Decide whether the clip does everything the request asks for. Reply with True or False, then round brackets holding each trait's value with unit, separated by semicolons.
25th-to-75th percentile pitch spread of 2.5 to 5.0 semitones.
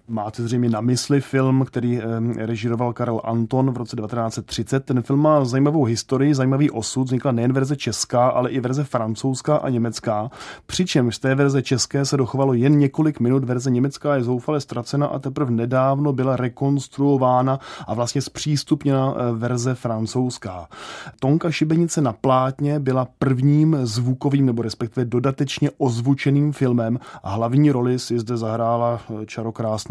True (2.8 semitones)